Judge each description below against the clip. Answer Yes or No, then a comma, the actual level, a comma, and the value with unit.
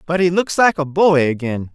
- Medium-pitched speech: Yes, medium, 160 Hz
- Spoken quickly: Yes, fast, 240 wpm